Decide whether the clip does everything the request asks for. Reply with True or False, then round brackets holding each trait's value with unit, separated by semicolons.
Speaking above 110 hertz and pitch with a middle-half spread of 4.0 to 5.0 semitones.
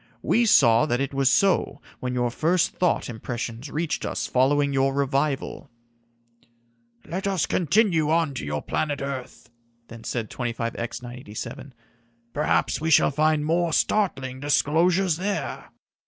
True (140 Hz; 4.7 semitones)